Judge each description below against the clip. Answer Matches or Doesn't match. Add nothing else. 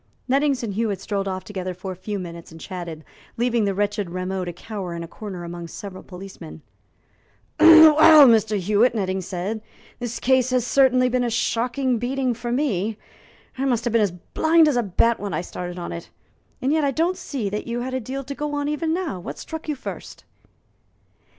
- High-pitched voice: Matches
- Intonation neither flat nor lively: Doesn't match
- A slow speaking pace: Doesn't match